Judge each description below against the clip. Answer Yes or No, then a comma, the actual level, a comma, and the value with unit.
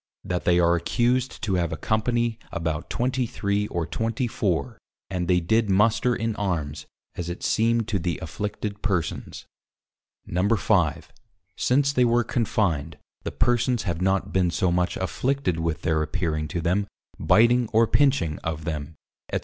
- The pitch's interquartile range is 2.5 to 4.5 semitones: No, average, 5.3 semitones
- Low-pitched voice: Yes, low, 100 Hz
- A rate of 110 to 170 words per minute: Yes, average, 150 wpm